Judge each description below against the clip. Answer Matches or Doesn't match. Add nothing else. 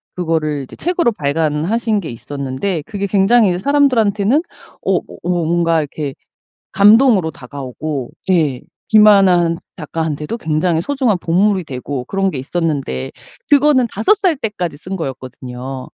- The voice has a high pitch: Doesn't match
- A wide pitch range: Matches